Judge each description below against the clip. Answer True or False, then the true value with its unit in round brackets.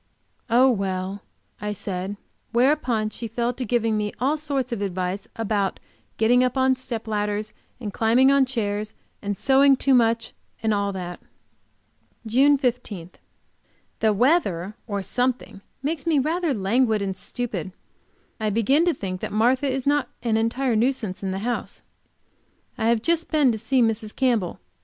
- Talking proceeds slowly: False (155 wpm)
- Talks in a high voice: True (230 Hz)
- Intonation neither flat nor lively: True (4.1 semitones)